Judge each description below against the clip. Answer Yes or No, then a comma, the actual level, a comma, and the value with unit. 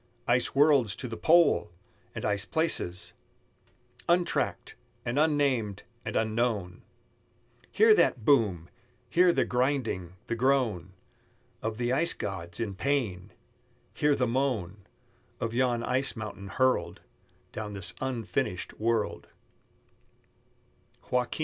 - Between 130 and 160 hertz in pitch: No, low, 115 Hz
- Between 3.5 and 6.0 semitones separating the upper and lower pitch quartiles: Yes, average, 5.2 semitones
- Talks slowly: Yes, slow, 110 wpm